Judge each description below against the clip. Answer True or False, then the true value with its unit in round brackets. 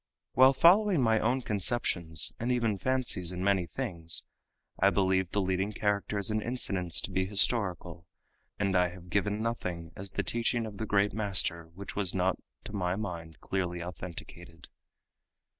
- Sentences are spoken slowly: False (160 wpm)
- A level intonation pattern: False (3.6 semitones)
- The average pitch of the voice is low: True (100 Hz)